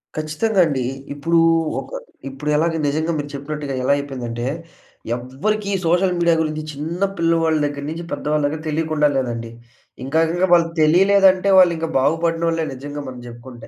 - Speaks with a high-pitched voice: No, medium, 155 Hz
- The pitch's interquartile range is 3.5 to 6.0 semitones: No, average, 3.0 semitones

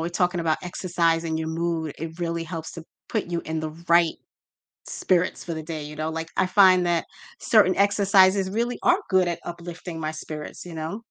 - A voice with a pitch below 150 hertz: No, medium, 170 Hz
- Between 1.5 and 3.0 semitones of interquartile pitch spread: Yes, narrow, 2.4 semitones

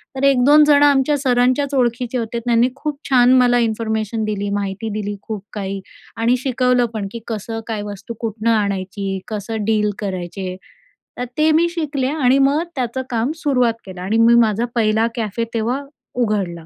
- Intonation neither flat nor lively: Yes, average, 3.4 semitones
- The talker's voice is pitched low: No, high, 230 Hz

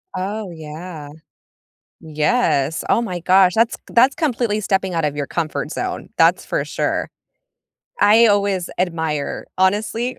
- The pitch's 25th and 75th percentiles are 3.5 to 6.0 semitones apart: Yes, average, 5.2 semitones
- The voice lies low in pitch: No, medium, 185 Hz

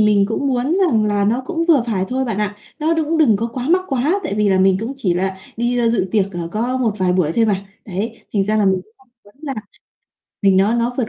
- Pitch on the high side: Yes, high, 220 Hz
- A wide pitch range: No, average, 4.6 semitones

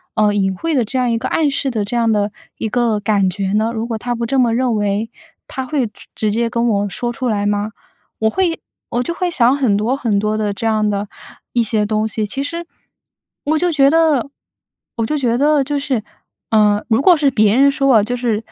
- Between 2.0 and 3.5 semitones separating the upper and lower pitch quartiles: No, average, 4.3 semitones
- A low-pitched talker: No, high, 230 Hz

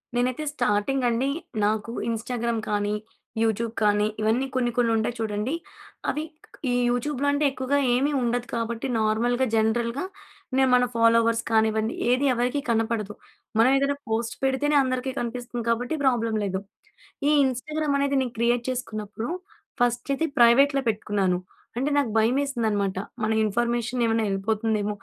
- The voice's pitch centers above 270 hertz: No, high, 235 Hz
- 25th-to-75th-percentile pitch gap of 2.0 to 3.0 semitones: Yes, average, 2.7 semitones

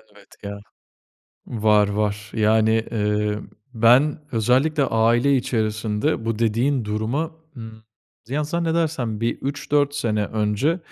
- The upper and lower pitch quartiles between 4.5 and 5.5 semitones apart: Yes, average, 4.8 semitones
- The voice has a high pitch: No, low, 115 Hz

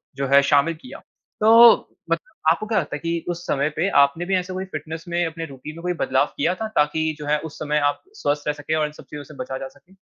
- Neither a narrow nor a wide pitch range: Yes, average, 3.2 semitones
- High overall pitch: No, medium, 155 Hz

